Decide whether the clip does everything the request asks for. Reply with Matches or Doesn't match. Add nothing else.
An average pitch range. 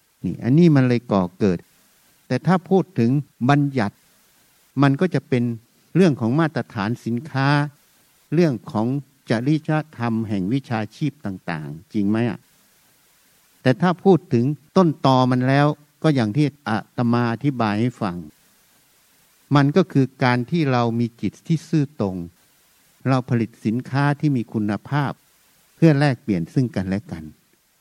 Matches